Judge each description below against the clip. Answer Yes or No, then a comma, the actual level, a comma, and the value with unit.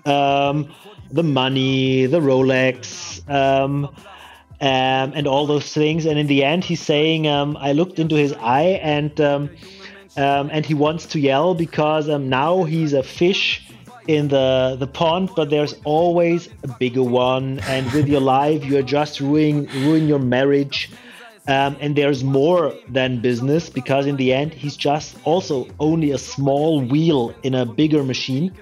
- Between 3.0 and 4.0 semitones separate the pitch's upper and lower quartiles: No, narrow, 2.5 semitones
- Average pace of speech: Yes, average, 165 wpm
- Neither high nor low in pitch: Yes, medium, 145 Hz